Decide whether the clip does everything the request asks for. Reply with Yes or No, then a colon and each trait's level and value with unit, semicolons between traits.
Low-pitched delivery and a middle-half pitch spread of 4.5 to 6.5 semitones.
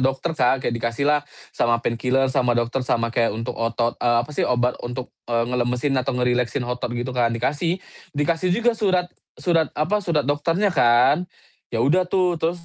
Yes: low, 130 Hz; average, 5.2 semitones